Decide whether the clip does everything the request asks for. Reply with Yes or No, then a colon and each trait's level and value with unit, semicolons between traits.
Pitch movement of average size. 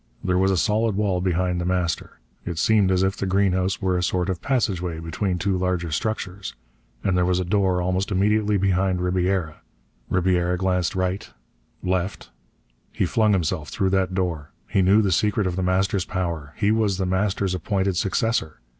No: narrow, 1.5 semitones